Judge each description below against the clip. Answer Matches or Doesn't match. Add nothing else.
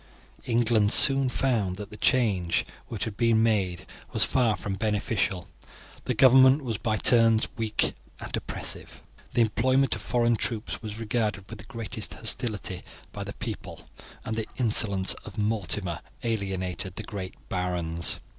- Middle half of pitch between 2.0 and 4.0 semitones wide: Matches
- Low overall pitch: Matches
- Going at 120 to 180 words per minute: Matches